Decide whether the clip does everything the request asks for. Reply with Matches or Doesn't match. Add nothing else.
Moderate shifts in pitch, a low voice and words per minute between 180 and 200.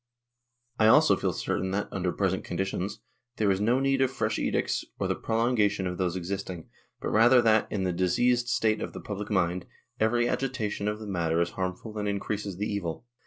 Matches